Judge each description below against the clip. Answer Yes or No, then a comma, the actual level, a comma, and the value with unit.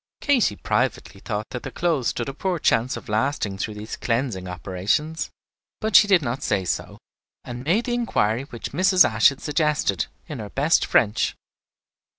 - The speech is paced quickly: No, average, 170 wpm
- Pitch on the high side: No, low, 130 Hz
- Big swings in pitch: Yes, wide, 7.1 semitones